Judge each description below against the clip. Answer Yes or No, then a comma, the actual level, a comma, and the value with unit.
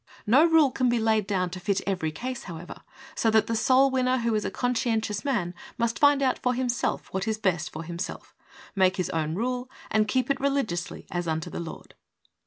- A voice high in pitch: Yes, high, 220 Hz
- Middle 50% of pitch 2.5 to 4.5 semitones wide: No, wide, 5.6 semitones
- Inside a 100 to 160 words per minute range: No, fast, 205 wpm